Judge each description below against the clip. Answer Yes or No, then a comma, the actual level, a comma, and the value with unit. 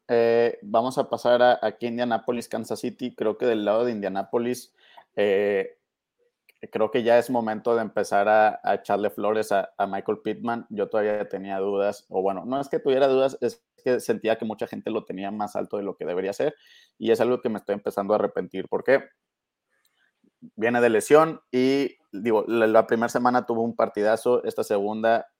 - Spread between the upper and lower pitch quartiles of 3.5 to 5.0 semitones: No, average, 2.9 semitones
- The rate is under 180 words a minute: No, fast, 190 wpm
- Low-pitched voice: Yes, low, 115 Hz